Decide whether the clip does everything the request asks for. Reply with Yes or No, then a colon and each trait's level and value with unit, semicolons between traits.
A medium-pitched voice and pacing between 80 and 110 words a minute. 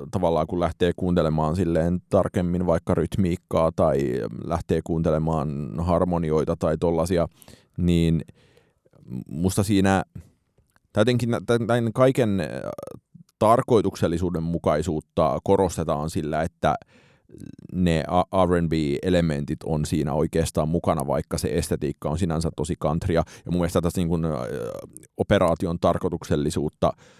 No: very low, 85 Hz; slow, 95 wpm